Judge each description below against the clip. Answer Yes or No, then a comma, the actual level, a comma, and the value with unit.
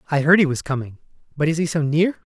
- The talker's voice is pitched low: No, medium, 155 Hz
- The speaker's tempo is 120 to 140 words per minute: No, fast, 260 wpm